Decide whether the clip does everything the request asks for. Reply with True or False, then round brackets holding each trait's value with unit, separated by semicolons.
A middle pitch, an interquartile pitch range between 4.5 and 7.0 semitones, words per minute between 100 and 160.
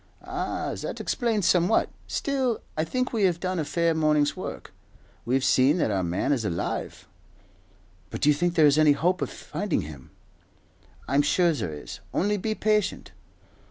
False (165 Hz; 5.2 semitones; 170 wpm)